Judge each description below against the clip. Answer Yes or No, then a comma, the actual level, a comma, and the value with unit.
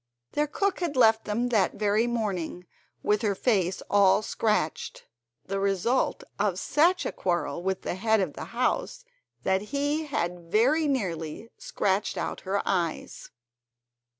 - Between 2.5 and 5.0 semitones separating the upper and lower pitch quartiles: No, wide, 5.4 semitones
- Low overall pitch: No, high, 210 Hz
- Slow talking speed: No, average, 145 wpm